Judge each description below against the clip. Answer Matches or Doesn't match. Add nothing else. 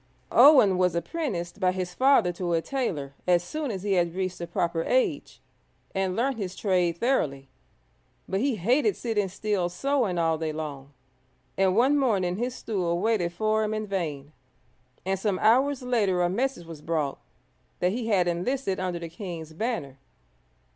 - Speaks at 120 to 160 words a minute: Doesn't match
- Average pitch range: Matches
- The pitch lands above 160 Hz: Matches